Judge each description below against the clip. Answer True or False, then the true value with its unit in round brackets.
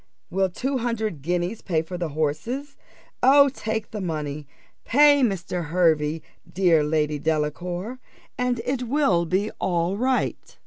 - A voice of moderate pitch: True (180 Hz)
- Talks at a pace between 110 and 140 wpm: True (135 wpm)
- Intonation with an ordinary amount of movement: False (7.4 semitones)